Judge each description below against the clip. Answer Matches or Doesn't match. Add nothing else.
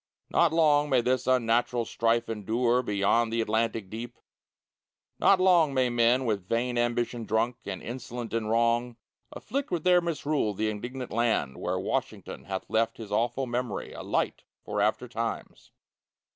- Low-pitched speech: Matches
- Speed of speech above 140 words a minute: Matches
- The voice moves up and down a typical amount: Doesn't match